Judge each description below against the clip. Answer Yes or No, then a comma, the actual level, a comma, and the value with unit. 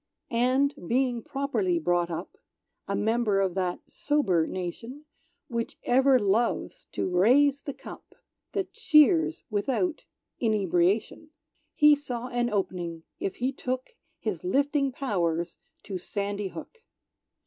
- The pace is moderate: No, slow, 120 wpm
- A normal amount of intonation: No, wide, 6.6 semitones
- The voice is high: Yes, high, 240 Hz